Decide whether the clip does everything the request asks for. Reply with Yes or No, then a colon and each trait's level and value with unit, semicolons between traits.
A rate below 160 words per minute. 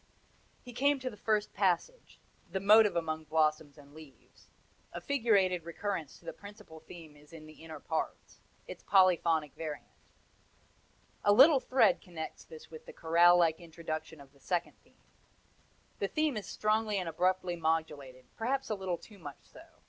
No: average, 165 wpm